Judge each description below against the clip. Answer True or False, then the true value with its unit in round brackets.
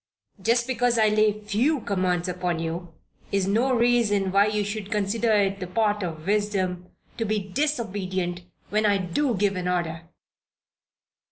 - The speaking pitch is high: True (205 Hz)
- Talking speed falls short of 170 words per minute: True (155 wpm)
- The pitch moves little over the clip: False (3.2 semitones)